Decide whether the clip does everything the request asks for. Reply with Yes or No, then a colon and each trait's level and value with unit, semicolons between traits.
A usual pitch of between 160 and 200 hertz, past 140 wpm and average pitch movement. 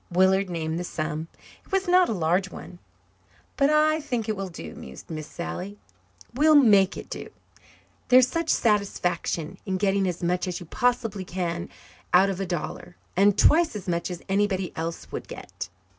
Yes: high, 190 Hz; average, 175 wpm; average, 4.7 semitones